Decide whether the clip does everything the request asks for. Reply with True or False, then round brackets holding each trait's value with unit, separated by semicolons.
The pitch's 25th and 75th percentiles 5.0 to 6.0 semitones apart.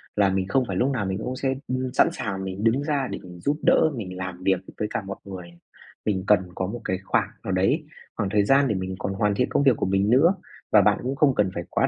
True (5.4 semitones)